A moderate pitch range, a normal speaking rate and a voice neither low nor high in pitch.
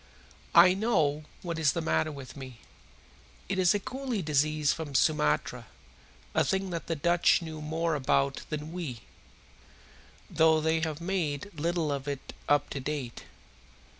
Yes: average, 3.1 semitones; average, 150 wpm; medium, 155 Hz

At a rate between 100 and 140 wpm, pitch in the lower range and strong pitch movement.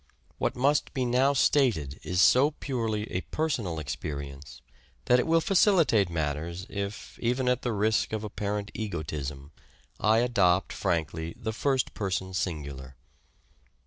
Yes: slow, 135 wpm; low, 100 Hz; wide, 7.4 semitones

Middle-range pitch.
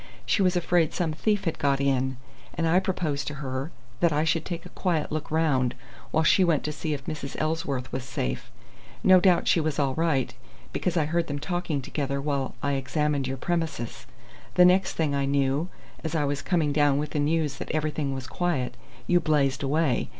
Yes: medium, 150 Hz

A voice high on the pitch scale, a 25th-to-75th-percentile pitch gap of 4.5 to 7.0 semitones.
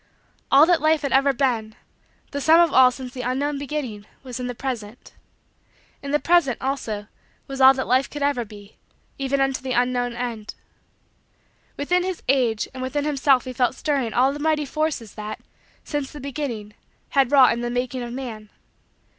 No: very high, 260 Hz; average, 2.8 semitones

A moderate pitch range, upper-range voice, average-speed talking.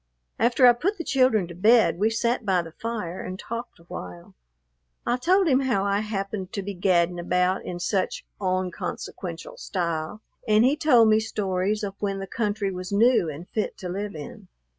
Yes: average, 4.3 semitones; high, 200 Hz; average, 185 wpm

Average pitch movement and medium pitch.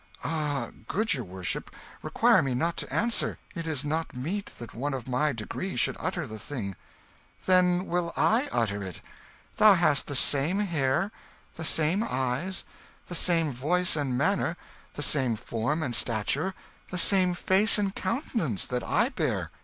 No: wide, 6.3 semitones; medium, 155 Hz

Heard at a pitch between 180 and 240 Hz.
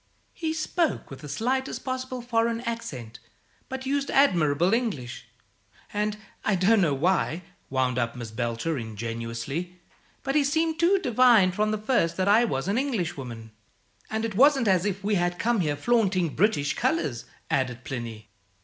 Yes: high, 190 Hz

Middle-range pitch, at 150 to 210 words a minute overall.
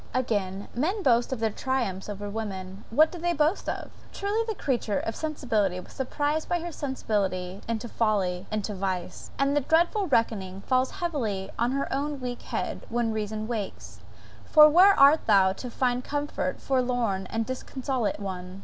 No: high, 240 Hz; average, 165 wpm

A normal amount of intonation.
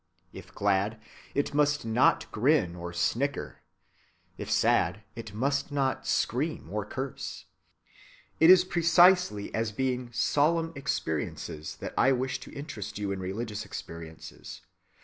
No: wide, 5.8 semitones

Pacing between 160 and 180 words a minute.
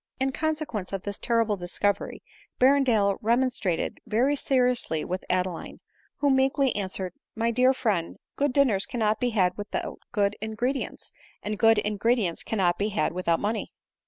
No: average, 150 wpm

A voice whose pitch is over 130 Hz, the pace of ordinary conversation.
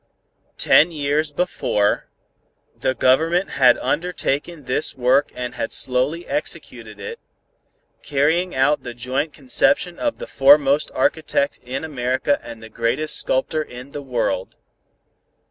No: medium, 140 Hz; slow, 125 wpm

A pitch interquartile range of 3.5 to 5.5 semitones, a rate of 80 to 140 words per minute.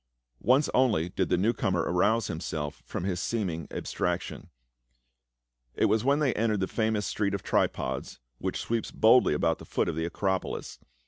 No: average, 4.6 semitones; average, 170 wpm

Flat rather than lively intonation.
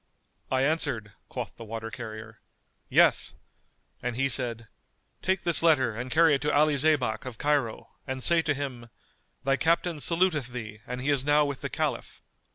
No: average, 4.2 semitones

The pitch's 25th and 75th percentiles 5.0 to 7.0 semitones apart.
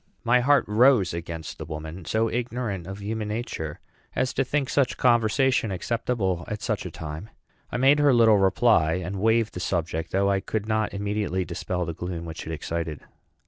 Yes: wide, 5.6 semitones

